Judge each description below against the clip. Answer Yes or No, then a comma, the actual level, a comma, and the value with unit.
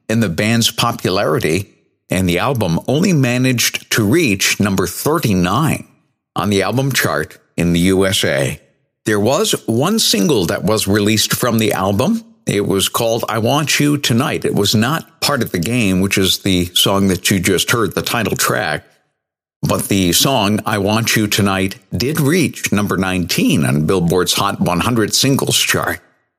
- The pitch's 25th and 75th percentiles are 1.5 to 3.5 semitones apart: No, average, 4.9 semitones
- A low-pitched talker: Yes, low, 110 Hz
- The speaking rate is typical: Yes, average, 165 wpm